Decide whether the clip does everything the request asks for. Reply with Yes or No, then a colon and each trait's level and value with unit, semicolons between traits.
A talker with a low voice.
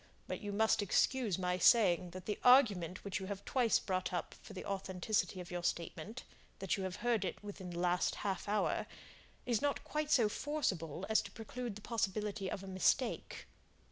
No: high, 200 Hz